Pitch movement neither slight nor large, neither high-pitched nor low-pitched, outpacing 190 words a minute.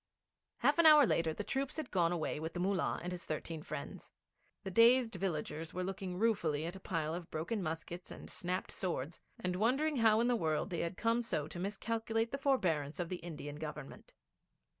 No: wide, 5.8 semitones; medium, 180 Hz; average, 200 wpm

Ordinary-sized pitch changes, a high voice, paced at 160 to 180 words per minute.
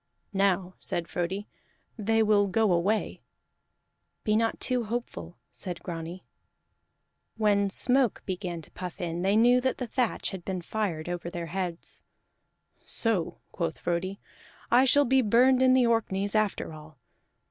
No: average, 4.5 semitones; high, 200 Hz; average, 145 wpm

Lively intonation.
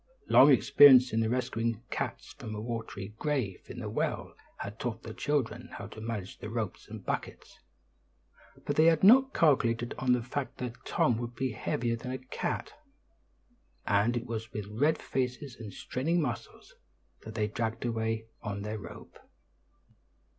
No: average, 2.7 semitones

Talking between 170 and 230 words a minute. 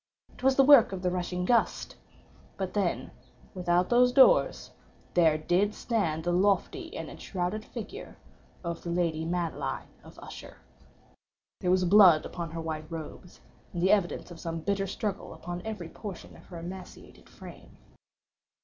No: average, 150 wpm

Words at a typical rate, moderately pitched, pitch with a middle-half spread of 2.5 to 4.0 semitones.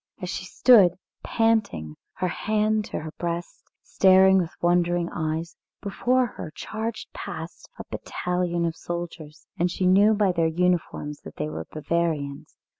Yes: average, 145 wpm; medium, 175 Hz; average, 3.2 semitones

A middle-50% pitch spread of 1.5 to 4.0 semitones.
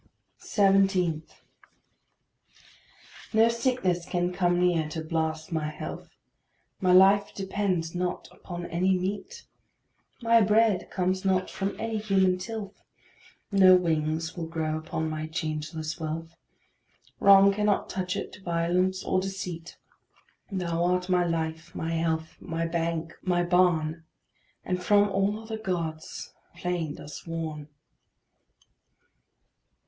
Yes: average, 2.9 semitones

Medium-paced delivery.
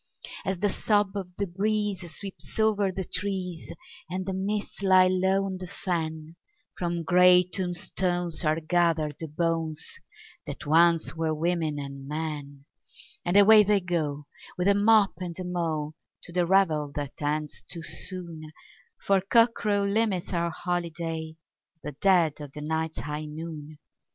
Yes: average, 145 wpm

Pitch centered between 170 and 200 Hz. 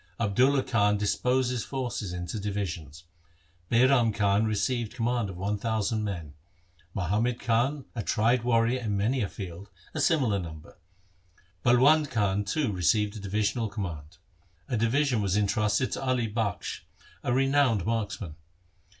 No: low, 110 Hz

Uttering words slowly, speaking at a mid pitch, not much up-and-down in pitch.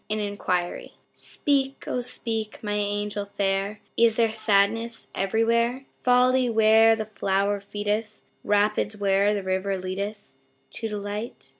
No: slow, 125 wpm; high, 210 Hz; narrow, 2.1 semitones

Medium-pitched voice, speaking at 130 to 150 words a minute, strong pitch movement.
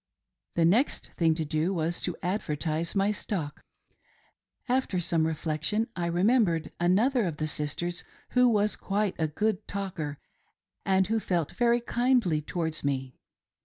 No: medium, 175 Hz; average, 140 wpm; average, 4.9 semitones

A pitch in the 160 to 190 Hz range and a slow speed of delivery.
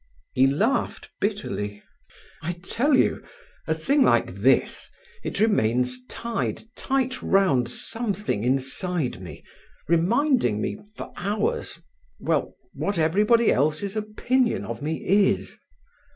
Yes: medium, 185 Hz; slow, 105 wpm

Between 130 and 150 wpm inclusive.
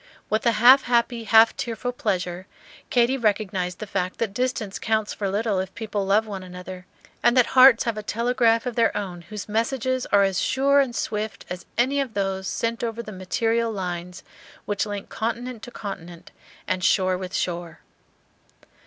No: average, 175 wpm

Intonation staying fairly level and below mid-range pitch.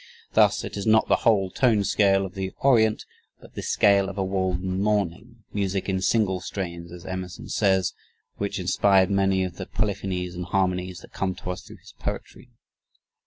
Yes: narrow, 1.7 semitones; very low, 95 Hz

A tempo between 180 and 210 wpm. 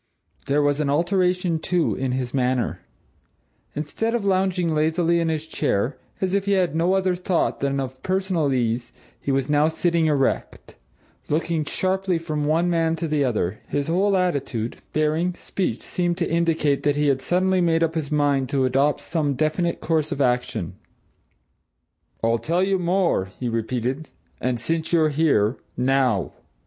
No: average, 165 wpm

